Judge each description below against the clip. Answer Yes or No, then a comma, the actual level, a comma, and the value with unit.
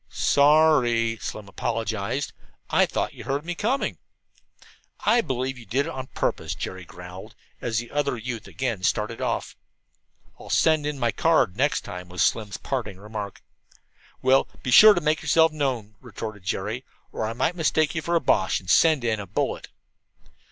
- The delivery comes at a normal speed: Yes, average, 170 wpm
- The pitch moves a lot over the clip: Yes, wide, 5.8 semitones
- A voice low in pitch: Yes, low, 125 Hz